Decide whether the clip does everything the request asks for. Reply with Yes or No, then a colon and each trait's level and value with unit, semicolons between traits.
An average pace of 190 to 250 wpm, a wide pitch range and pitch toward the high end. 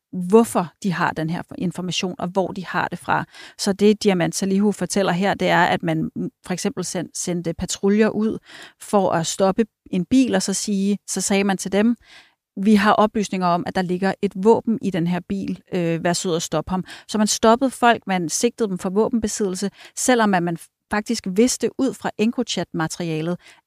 No: average, 195 wpm; average, 3.2 semitones; high, 195 Hz